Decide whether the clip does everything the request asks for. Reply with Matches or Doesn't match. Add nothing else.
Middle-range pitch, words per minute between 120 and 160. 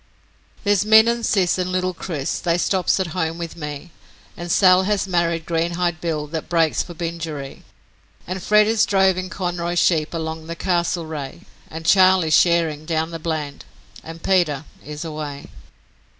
Matches